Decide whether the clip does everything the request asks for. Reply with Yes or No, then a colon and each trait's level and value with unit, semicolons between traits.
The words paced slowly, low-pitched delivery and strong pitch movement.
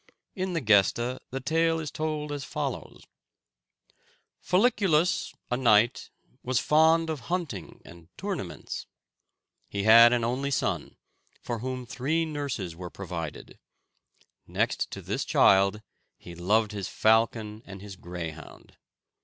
Yes: slow, 125 wpm; low, 120 Hz; wide, 7.5 semitones